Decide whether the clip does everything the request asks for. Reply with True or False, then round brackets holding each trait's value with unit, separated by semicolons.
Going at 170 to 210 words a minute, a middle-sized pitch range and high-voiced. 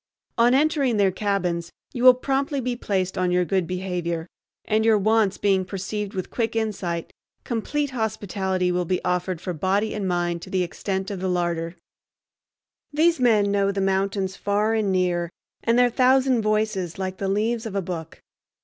True (175 wpm; 3.6 semitones; 195 Hz)